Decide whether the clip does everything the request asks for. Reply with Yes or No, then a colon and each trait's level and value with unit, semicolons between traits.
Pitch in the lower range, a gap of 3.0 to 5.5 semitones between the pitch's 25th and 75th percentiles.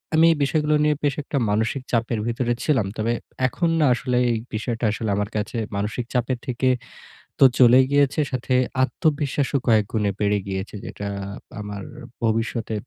Yes: low, 120 Hz; average, 4.3 semitones